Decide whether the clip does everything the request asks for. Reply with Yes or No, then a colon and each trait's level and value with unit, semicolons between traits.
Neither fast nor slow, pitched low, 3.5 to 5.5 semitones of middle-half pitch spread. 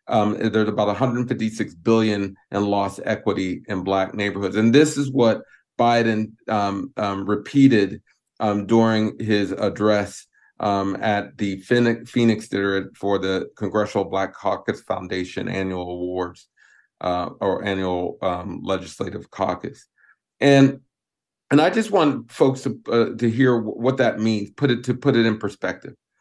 No: average, 145 wpm; low, 105 Hz; average, 3.1 semitones